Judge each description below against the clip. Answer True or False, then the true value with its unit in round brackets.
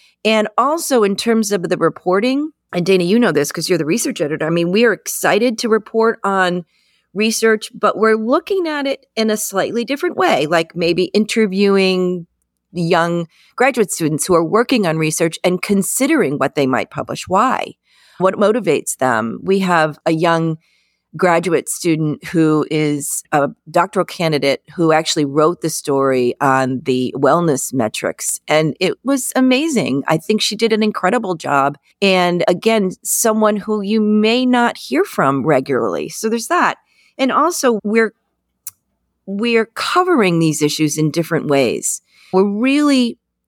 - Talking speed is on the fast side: False (155 wpm)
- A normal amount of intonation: False (5.8 semitones)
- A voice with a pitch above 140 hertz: True (190 Hz)